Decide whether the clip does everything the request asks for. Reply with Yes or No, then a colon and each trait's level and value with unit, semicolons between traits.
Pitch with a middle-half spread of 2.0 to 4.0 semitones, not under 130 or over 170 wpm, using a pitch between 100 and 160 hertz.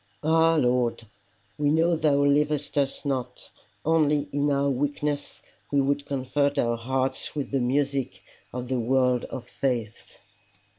Yes: narrow, 2.5 semitones; average, 140 wpm; medium, 140 Hz